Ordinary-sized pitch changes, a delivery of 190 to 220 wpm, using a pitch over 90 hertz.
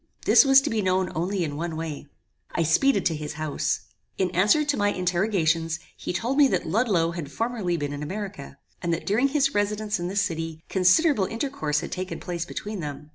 Yes: average, 4.7 semitones; average, 200 wpm; medium, 185 Hz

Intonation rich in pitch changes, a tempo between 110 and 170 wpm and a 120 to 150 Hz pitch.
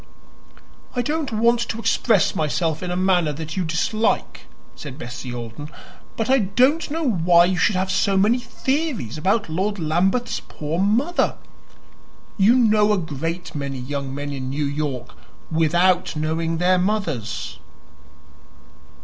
No: wide, 6.0 semitones; average, 140 wpm; medium, 180 Hz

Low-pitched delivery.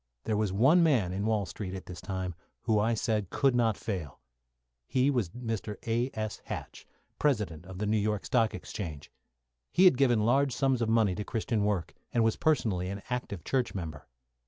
Yes: low, 110 Hz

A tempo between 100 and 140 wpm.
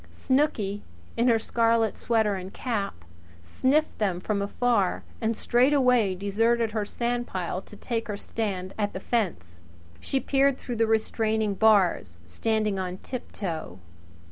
Yes: slow, 135 wpm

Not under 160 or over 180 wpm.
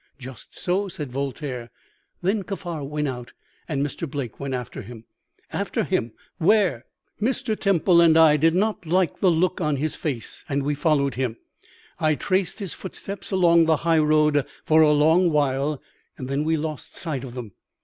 Yes: average, 175 wpm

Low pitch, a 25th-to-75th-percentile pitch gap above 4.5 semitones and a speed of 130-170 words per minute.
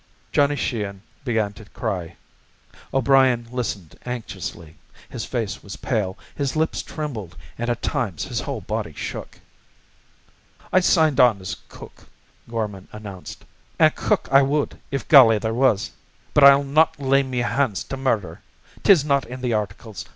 Yes: low, 120 Hz; average, 5.0 semitones; average, 150 wpm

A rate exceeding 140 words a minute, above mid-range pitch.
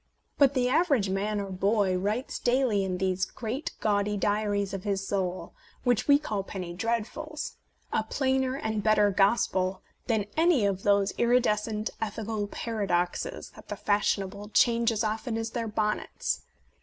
Yes: average, 150 wpm; high, 210 Hz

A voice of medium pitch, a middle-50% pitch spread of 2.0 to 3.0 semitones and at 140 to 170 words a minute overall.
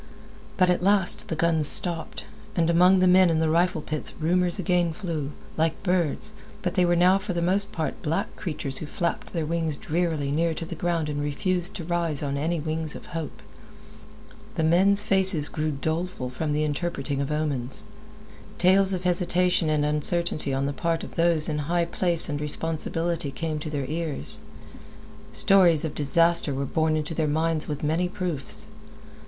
No: medium, 165 Hz; average, 2.7 semitones; average, 180 wpm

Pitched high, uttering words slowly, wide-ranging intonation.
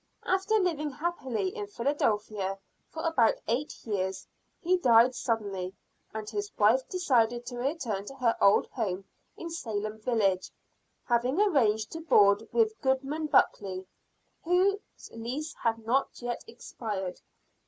Yes: high, 240 Hz; slow, 130 wpm; wide, 6.5 semitones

